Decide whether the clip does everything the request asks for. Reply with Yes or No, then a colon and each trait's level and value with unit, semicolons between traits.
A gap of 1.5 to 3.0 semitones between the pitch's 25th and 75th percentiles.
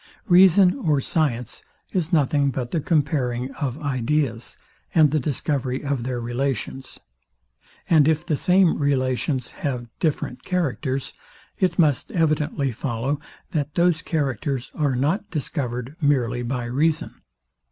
No: average, 3.7 semitones